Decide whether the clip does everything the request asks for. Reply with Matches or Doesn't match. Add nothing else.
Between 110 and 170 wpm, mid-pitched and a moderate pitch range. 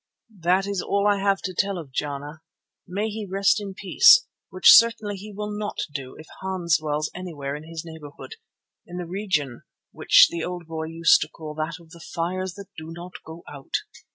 Doesn't match